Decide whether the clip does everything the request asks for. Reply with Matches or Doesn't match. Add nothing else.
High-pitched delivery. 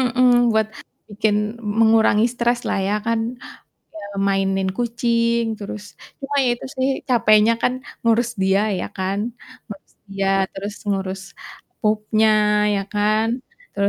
Matches